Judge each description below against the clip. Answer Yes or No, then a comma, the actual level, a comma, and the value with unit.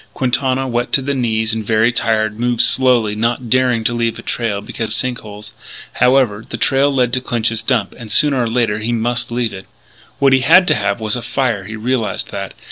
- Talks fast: Yes, fast, 215 wpm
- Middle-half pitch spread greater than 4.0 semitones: No, narrow, 2.6 semitones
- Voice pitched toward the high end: No, low, 120 Hz